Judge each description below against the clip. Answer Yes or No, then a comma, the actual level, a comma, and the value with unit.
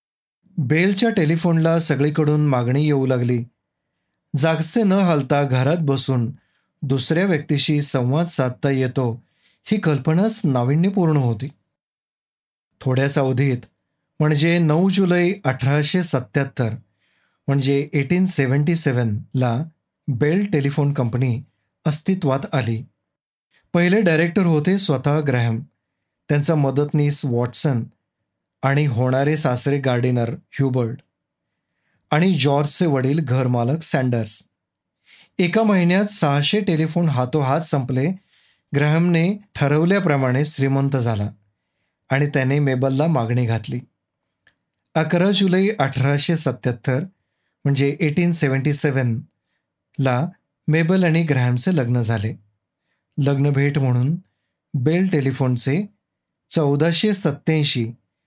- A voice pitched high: No, medium, 145 Hz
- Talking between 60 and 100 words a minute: Yes, average, 90 wpm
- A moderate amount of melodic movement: Yes, average, 4.1 semitones